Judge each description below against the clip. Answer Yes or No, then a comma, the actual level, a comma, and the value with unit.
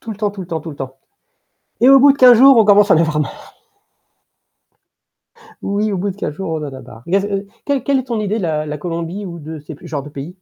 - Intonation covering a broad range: Yes, wide, 5.7 semitones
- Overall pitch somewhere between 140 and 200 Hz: Yes, high, 190 Hz